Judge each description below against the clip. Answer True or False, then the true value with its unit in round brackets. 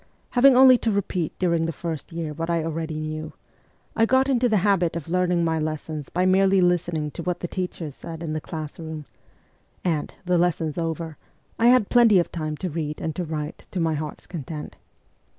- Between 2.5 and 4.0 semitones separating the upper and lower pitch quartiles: True (2.8 semitones)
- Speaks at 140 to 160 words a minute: False (200 wpm)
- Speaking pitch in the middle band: True (170 Hz)